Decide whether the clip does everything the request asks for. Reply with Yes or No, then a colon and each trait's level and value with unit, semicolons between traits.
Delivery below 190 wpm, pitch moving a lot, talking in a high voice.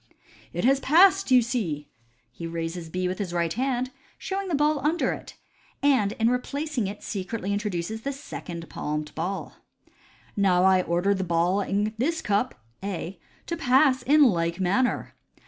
Yes: average, 170 wpm; wide, 7.1 semitones; high, 205 Hz